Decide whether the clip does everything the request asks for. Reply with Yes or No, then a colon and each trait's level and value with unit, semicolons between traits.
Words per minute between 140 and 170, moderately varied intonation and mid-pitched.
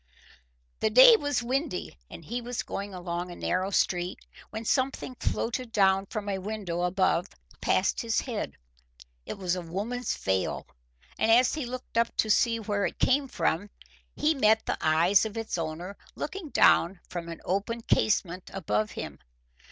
No: average, 165 wpm; average, 5.0 semitones; high, 205 Hz